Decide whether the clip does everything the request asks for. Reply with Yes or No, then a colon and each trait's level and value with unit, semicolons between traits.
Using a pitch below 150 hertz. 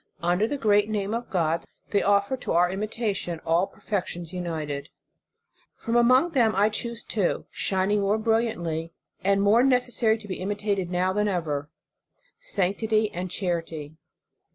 No: high, 200 Hz